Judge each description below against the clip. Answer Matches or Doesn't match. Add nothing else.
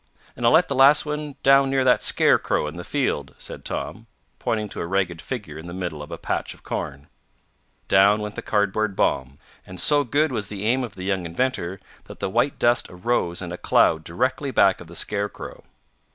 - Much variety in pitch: Matches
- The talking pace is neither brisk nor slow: Doesn't match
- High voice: Doesn't match